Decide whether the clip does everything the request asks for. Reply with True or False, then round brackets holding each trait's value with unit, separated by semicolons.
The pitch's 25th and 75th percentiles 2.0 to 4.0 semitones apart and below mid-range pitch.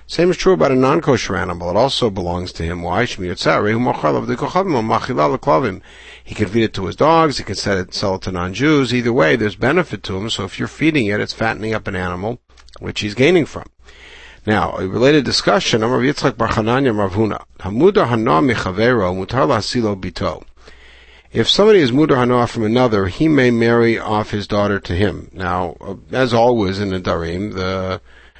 False (4.7 semitones; 110 Hz)